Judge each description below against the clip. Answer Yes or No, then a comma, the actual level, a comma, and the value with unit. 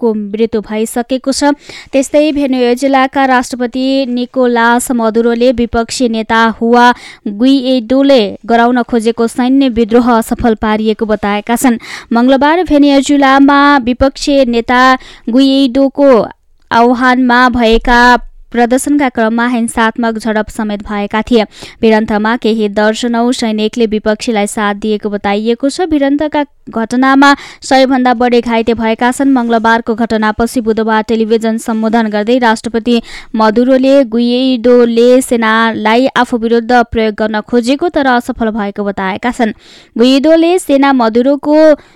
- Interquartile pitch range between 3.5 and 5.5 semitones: No, average, 2.8 semitones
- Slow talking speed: Yes, slow, 105 wpm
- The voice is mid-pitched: No, high, 240 Hz